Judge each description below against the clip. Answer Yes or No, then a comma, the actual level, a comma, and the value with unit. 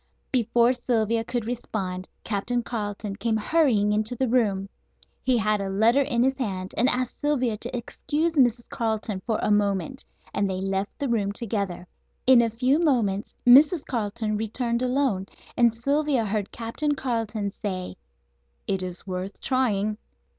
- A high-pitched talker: Yes, high, 225 Hz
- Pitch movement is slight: No, average, 3.7 semitones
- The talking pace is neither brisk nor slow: Yes, average, 155 wpm